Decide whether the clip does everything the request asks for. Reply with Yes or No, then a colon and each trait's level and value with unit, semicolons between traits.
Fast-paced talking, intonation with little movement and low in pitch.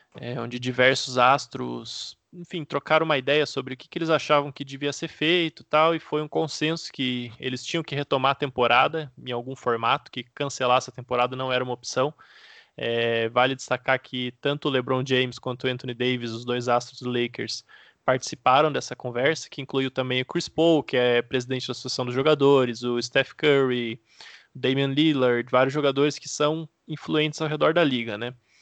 No: fast, 190 wpm; average, 3.1 semitones; low, 130 Hz